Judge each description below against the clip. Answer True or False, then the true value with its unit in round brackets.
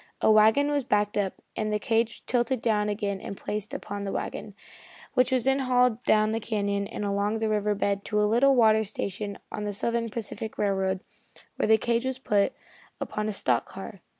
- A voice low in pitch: False (215 Hz)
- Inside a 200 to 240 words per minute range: True (205 wpm)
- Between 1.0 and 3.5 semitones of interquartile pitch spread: True (2.4 semitones)